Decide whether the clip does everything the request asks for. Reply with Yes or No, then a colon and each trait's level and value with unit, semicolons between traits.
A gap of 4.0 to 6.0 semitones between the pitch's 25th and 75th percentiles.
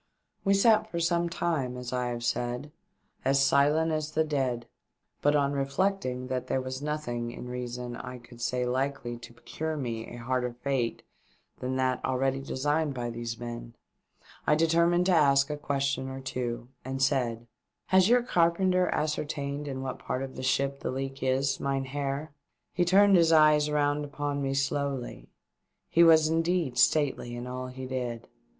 No: average, 3.4 semitones